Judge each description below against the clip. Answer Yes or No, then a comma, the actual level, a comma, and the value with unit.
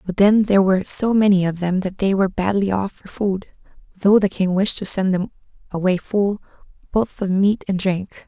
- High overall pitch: Yes, high, 195 Hz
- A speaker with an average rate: No, fast, 210 wpm